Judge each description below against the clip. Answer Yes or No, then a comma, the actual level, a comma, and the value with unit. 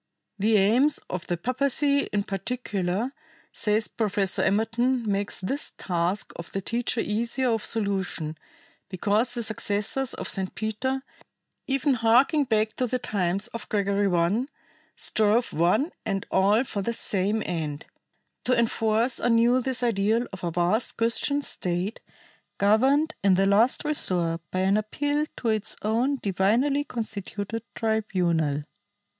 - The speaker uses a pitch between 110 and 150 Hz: No, high, 215 Hz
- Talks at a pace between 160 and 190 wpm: No, slow, 135 wpm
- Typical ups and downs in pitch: Yes, average, 4.0 semitones